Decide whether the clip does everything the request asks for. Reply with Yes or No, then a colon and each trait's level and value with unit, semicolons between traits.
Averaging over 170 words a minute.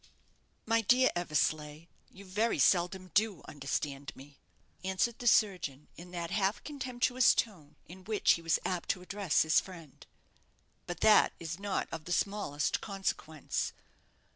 No: average, 140 wpm